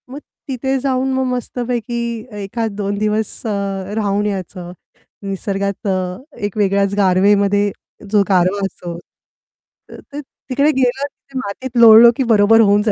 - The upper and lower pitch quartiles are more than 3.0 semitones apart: Yes, average, 3.9 semitones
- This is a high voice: Yes, high, 210 Hz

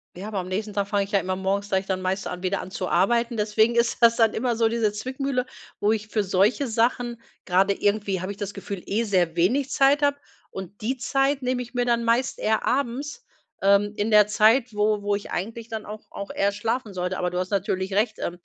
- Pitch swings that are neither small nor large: Yes, average, 3.2 semitones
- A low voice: No, high, 210 Hz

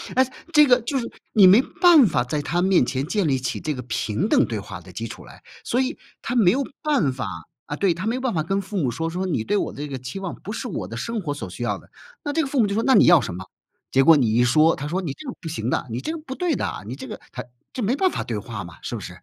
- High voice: No, medium, 175 Hz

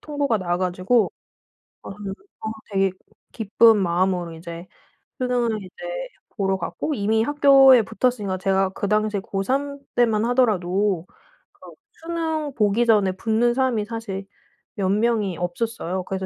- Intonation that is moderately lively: Yes, average, 4.1 semitones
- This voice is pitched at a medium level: No, high, 210 Hz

